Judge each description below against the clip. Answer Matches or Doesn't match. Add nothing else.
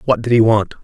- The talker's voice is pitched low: Matches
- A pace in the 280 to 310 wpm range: Matches